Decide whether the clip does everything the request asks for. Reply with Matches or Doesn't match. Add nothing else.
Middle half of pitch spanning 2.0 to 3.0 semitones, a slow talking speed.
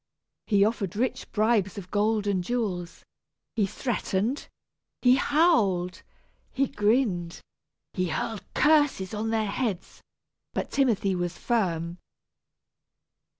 Doesn't match